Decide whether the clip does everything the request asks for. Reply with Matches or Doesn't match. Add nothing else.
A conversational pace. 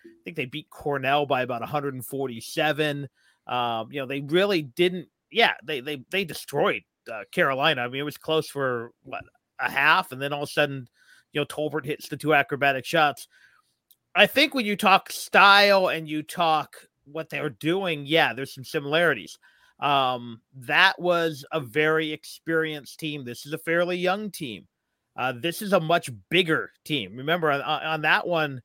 Matches